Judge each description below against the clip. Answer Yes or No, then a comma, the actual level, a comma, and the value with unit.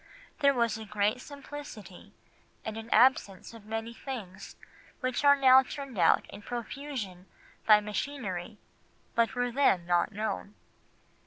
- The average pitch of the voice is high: Yes, high, 225 Hz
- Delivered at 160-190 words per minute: No, slow, 135 wpm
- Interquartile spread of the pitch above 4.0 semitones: Yes, average, 4.4 semitones